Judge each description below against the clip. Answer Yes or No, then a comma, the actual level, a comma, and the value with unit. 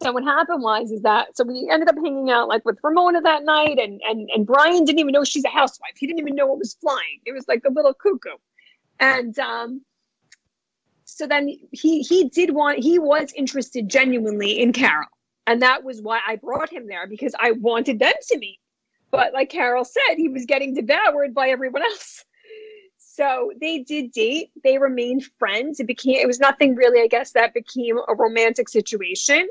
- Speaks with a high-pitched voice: Yes, very high, 270 Hz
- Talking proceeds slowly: No, average, 200 wpm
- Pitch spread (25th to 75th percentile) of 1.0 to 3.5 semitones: No, average, 4.2 semitones